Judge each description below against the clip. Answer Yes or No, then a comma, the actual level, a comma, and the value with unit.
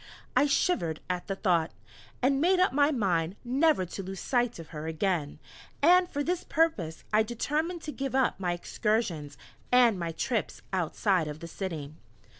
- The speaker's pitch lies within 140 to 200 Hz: No, high, 210 Hz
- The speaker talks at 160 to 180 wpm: Yes, average, 170 wpm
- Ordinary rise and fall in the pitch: No, wide, 8.8 semitones